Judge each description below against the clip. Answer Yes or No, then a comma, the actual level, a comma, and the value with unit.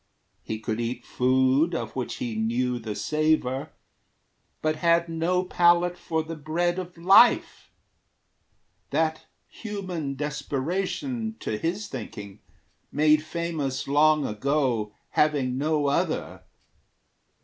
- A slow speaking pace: Yes, slow, 110 wpm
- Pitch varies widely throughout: No, average, 4.7 semitones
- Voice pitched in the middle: Yes, medium, 155 Hz